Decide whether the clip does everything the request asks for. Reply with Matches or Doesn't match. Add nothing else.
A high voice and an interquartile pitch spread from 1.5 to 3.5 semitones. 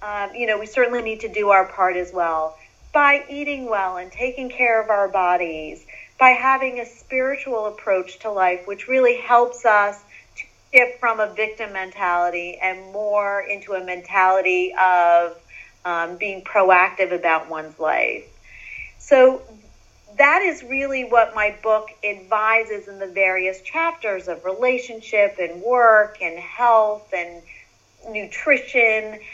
Doesn't match